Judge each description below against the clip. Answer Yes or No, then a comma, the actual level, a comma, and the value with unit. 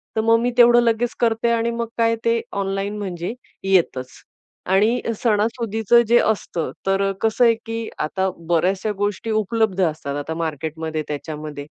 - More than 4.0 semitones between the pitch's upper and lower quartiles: Yes, average, 4.9 semitones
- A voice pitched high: Yes, high, 210 Hz